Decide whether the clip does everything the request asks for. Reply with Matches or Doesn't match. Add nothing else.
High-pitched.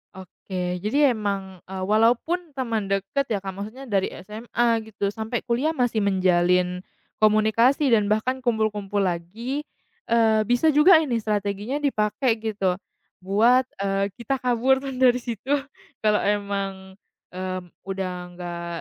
Matches